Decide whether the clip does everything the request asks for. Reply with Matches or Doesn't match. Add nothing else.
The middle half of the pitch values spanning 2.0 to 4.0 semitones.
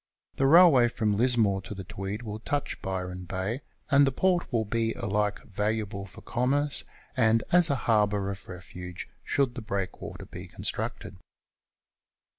Doesn't match